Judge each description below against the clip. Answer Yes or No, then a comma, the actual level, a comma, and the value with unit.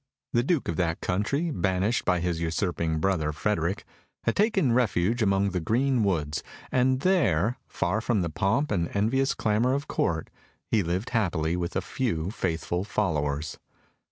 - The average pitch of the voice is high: No, very low, 95 Hz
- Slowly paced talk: No, average, 155 wpm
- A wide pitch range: Yes, wide, 6.1 semitones